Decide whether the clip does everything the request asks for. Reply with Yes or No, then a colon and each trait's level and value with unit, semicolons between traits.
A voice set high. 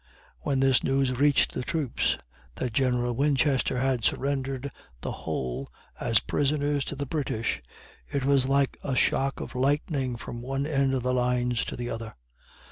No: low, 135 Hz